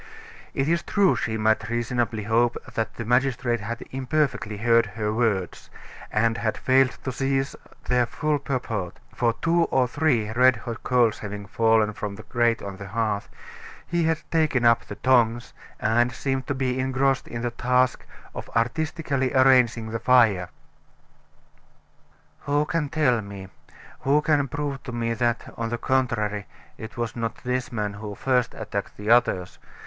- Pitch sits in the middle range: No, low, 120 Hz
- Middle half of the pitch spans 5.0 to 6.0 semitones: No, average, 3.0 semitones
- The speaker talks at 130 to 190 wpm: Yes, average, 160 wpm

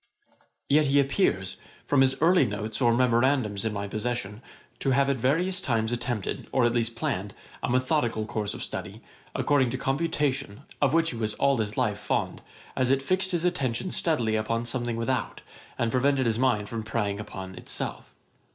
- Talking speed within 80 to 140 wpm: No, average, 180 wpm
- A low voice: Yes, low, 120 Hz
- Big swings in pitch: No, average, 4.0 semitones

